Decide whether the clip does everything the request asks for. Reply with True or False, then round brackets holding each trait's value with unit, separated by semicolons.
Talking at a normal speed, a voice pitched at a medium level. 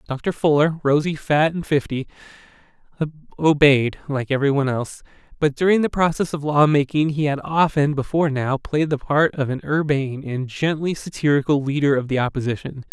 True (165 wpm; 145 Hz)